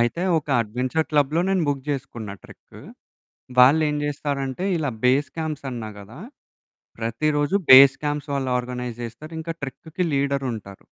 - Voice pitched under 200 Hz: Yes, medium, 140 Hz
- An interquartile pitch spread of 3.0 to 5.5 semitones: Yes, average, 3.5 semitones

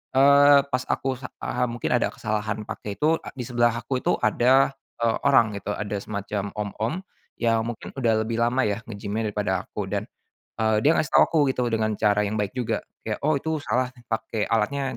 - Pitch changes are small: No, average, 3.6 semitones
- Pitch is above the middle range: No, low, 115 Hz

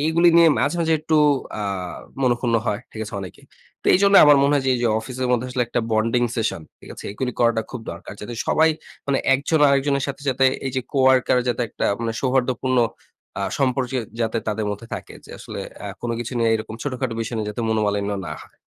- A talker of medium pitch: No, low, 125 Hz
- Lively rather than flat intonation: No, average, 3.4 semitones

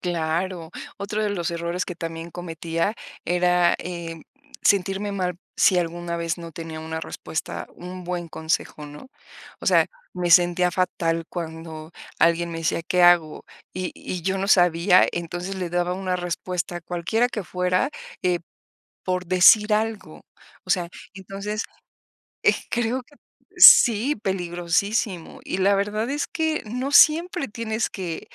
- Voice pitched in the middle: Yes, medium, 180 Hz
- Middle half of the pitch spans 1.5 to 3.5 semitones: Yes, average, 2.9 semitones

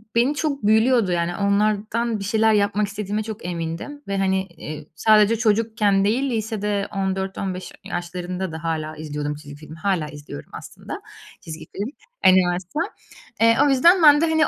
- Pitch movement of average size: Yes, average, 4.2 semitones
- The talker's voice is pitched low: No, high, 200 Hz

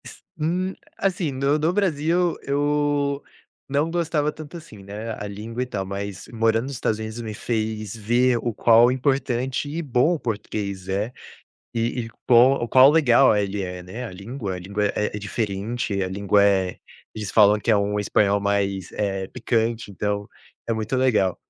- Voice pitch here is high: No, low, 115 Hz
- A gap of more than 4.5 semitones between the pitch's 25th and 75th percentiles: Yes, average, 5.2 semitones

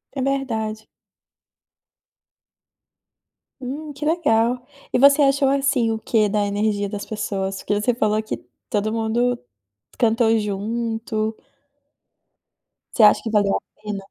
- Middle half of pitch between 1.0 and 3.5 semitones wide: Yes, average, 3.0 semitones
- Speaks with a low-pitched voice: No, high, 225 Hz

